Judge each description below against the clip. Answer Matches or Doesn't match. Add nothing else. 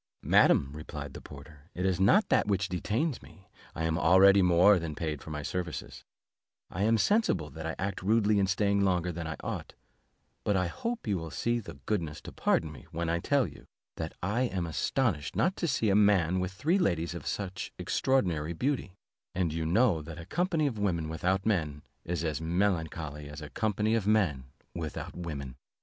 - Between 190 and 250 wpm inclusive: Matches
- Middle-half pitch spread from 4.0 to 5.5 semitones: Matches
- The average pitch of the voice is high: Doesn't match